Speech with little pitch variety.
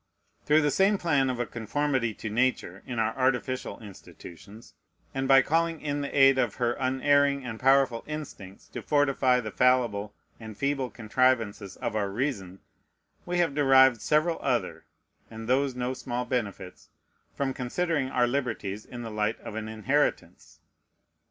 No: average, 3.9 semitones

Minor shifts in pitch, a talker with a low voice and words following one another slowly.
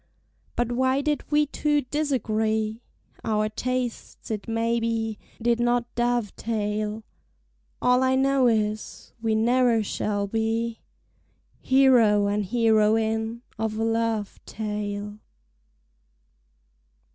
No: narrow, 2.2 semitones; high, 225 Hz; slow, 100 wpm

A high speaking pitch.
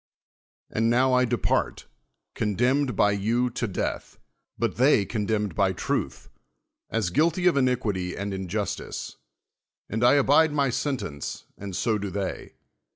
No: low, 115 Hz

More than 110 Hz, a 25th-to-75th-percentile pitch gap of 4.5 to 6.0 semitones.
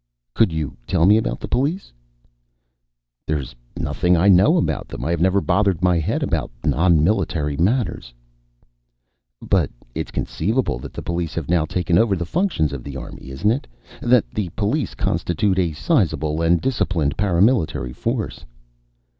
No: very low, 90 Hz; average, 5.0 semitones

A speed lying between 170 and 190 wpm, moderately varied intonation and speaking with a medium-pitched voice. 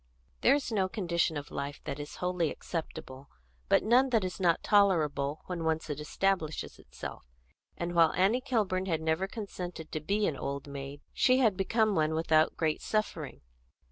Yes: average, 175 wpm; average, 4.6 semitones; medium, 170 Hz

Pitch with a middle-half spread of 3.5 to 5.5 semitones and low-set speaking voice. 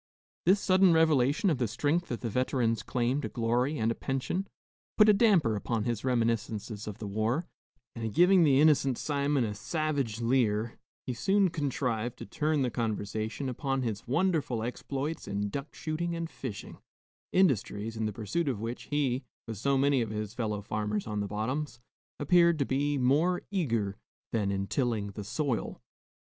Yes: average, 5.2 semitones; low, 125 Hz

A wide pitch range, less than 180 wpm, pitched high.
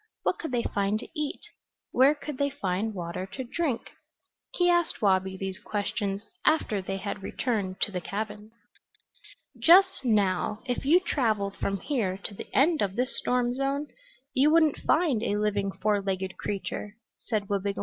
Yes: wide, 5.7 semitones; average, 165 wpm; high, 215 Hz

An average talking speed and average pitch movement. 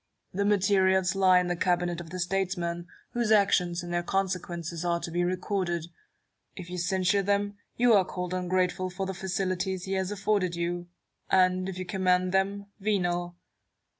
No: average, 165 wpm; narrow, 1.6 semitones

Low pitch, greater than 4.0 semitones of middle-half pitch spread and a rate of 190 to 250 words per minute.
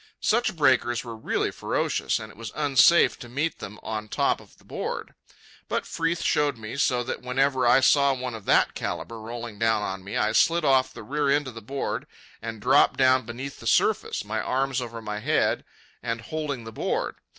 No: low, 125 Hz; average, 3.6 semitones; average, 200 wpm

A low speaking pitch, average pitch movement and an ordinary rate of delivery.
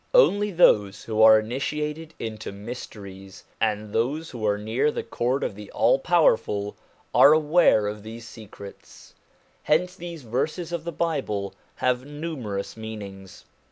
No: low, 115 Hz; wide, 6.7 semitones; average, 145 wpm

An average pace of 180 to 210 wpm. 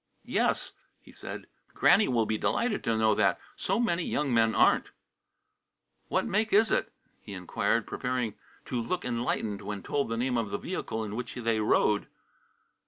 No: average, 170 wpm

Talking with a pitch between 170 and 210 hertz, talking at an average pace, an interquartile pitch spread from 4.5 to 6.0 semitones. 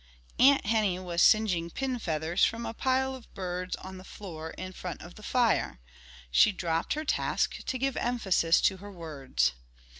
Yes: high, 190 Hz; average, 175 wpm; wide, 5.5 semitones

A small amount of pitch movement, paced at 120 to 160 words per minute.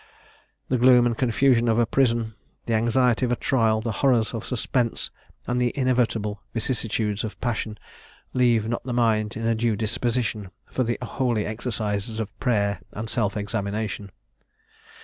Yes: narrow, 2.2 semitones; average, 155 wpm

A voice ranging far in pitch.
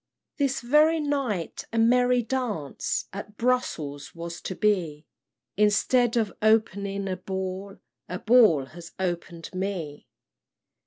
Yes: wide, 5.7 semitones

